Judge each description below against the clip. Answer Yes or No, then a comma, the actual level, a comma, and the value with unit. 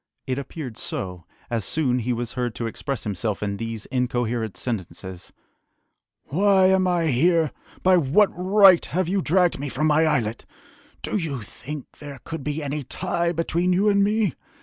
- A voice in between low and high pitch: Yes, medium, 145 Hz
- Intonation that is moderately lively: No, wide, 6.9 semitones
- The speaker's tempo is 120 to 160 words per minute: No, average, 170 wpm